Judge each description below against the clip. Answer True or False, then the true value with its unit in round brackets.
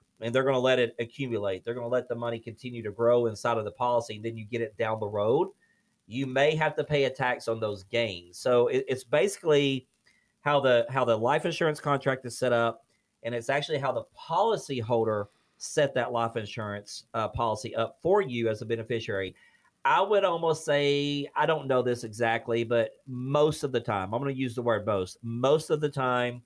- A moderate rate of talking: False (220 wpm)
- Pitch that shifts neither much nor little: True (3.2 semitones)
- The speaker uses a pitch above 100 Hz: True (120 Hz)